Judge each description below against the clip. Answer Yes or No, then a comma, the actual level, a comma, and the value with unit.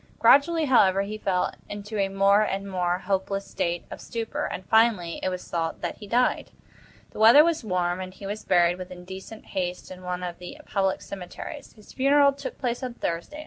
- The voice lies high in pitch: Yes, high, 195 Hz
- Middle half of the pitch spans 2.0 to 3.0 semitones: No, average, 3.8 semitones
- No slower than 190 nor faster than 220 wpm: Yes, average, 195 wpm